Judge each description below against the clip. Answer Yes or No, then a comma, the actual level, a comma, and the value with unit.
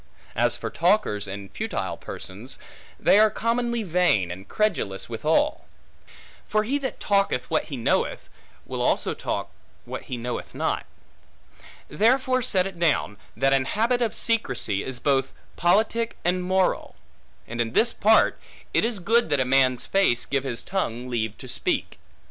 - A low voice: No, medium, 175 Hz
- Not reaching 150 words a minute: No, average, 155 wpm